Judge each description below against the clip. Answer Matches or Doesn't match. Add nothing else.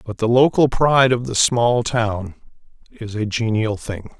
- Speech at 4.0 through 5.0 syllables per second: Matches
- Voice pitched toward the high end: Doesn't match